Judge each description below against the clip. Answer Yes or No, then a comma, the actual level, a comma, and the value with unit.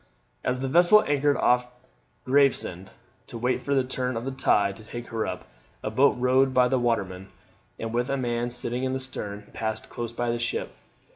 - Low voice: Yes, low, 125 Hz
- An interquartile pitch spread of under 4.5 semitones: Yes, narrow, 2.5 semitones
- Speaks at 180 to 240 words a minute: Yes, average, 200 wpm